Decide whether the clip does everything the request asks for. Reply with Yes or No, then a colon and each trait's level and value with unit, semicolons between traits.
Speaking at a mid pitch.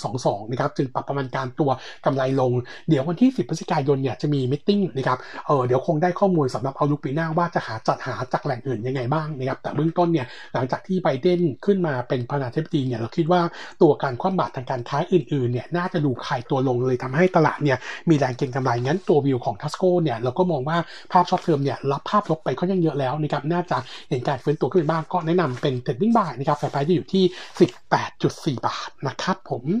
Yes: medium, 150 Hz